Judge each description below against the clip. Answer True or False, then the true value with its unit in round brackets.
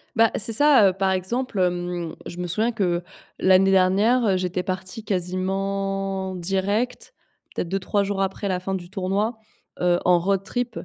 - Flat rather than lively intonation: True (1.9 semitones)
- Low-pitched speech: False (195 Hz)